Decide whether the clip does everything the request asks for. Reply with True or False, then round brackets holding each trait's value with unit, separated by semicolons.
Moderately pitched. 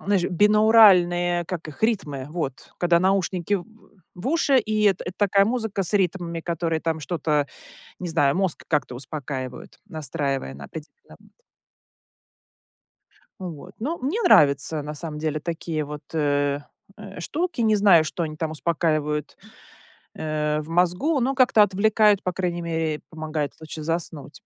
True (170 Hz)